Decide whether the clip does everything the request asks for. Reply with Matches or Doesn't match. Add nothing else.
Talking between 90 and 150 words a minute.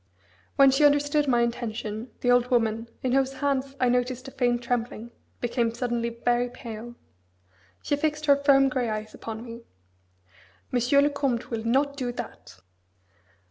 Doesn't match